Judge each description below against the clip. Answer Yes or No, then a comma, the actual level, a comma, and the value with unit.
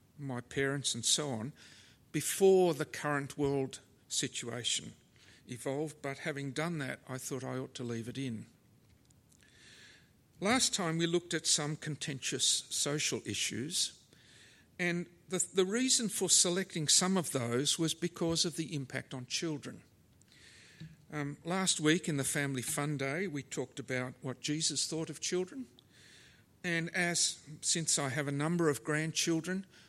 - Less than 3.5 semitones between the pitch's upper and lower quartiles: No, average, 3.9 semitones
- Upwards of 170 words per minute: No, average, 145 wpm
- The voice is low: No, medium, 150 Hz